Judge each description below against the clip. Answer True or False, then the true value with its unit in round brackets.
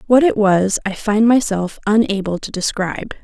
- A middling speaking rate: True (165 wpm)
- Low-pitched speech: False (210 Hz)